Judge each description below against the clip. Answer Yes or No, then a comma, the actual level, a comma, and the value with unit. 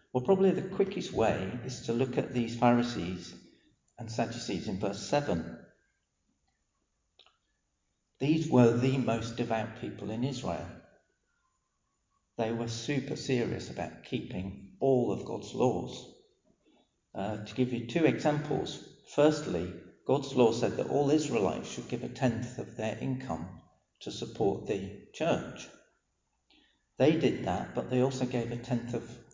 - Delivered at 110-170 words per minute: Yes, average, 140 wpm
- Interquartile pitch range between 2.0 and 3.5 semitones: Yes, average, 2.9 semitones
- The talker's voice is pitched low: Yes, low, 120 Hz